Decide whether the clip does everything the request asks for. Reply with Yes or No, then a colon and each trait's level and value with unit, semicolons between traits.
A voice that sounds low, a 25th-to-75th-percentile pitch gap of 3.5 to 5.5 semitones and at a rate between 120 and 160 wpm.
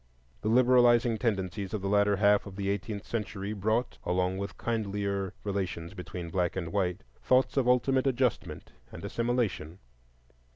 Yes: low, 100 Hz; average, 3.8 semitones; average, 150 wpm